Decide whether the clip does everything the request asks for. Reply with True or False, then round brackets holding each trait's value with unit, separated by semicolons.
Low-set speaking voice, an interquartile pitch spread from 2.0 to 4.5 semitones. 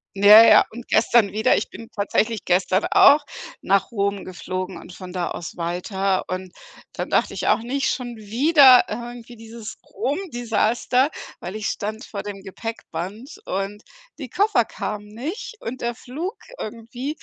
False (220 Hz; 3.7 semitones)